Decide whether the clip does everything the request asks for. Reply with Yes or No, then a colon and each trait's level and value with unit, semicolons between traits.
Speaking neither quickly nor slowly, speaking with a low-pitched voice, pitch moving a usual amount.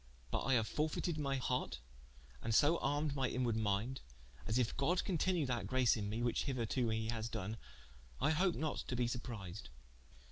Yes: average, 180 wpm; low, 125 Hz; average, 4.5 semitones